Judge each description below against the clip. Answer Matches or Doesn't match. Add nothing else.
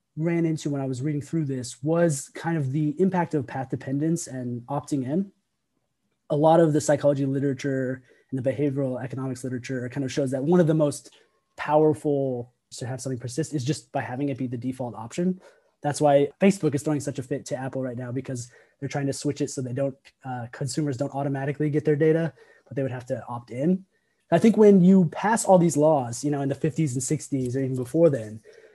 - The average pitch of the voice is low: Doesn't match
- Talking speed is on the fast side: Matches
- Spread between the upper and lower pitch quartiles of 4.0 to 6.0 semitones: Doesn't match